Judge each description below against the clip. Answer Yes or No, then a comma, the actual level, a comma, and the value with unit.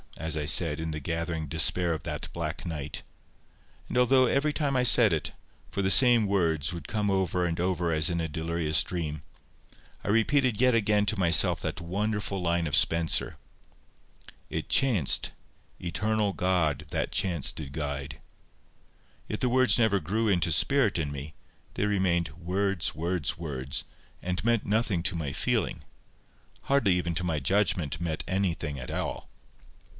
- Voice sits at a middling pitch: No, very low, 90 Hz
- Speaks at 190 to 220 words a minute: No, average, 150 wpm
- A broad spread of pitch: No, average, 4.6 semitones